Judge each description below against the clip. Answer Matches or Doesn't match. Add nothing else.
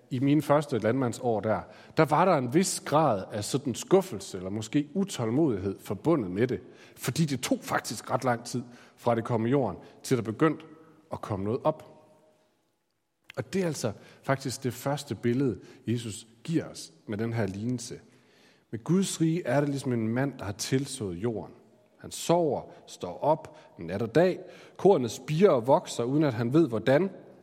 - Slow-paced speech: Doesn't match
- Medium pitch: Doesn't match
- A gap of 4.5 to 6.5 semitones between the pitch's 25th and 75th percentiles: Matches